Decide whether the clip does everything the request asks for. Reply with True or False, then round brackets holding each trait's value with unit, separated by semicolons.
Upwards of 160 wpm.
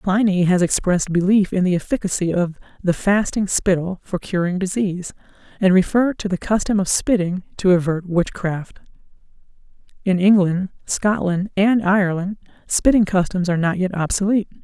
False (145 wpm)